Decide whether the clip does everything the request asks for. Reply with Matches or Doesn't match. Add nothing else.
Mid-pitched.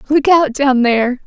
Doesn't match